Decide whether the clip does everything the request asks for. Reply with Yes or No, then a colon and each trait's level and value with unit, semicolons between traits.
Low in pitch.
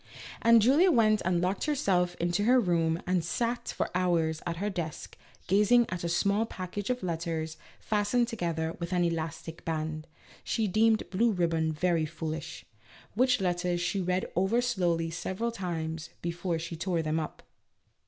No: medium, 180 Hz